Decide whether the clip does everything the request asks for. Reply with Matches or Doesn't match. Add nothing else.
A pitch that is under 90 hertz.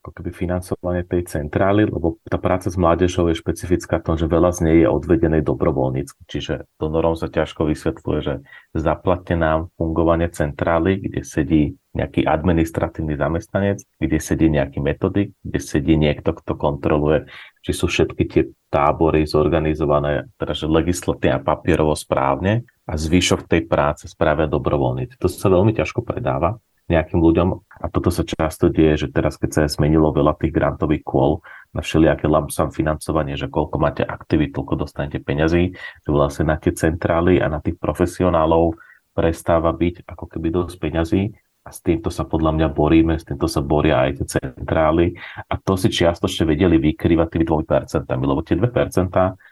Matches